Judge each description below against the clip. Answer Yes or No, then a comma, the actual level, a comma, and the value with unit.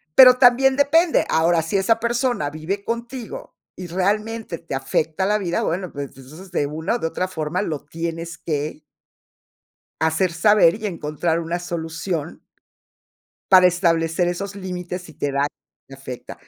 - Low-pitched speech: No, medium, 175 Hz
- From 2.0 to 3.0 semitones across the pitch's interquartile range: No, average, 4.3 semitones